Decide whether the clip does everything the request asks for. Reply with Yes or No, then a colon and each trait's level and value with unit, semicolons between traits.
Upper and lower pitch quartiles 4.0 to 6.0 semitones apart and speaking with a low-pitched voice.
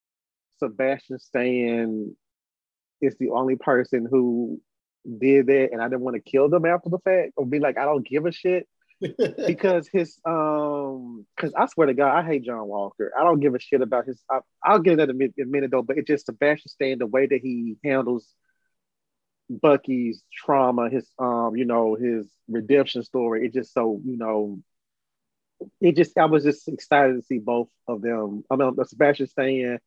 No: average, 3.5 semitones; low, 130 Hz